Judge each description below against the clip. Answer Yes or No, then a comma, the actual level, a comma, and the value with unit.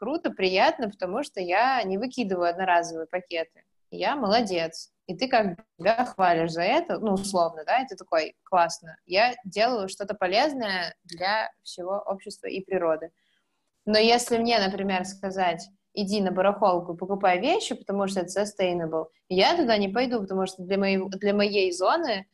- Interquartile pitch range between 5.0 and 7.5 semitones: No, average, 3.2 semitones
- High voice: Yes, high, 195 Hz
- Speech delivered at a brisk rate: No, average, 150 wpm